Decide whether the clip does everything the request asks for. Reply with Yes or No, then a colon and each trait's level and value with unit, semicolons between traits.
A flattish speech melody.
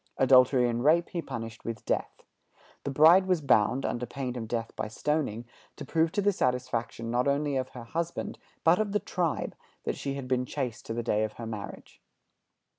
No: average, 4.8 semitones